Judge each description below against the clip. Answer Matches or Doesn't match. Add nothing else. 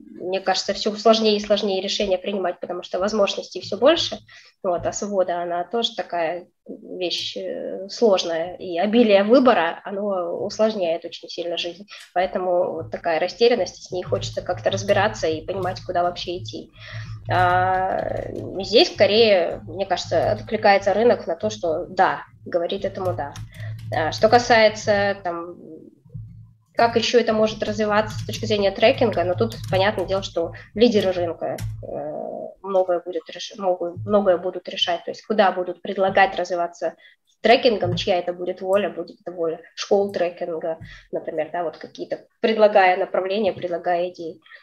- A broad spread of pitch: Doesn't match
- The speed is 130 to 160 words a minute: Matches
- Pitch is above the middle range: Doesn't match